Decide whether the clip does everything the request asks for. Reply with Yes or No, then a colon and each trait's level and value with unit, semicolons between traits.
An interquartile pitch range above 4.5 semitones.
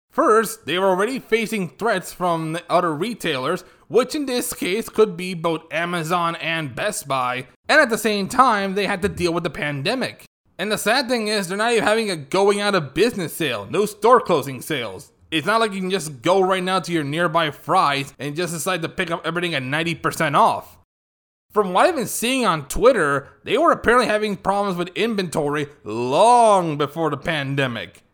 Yes: average, 4.9 semitones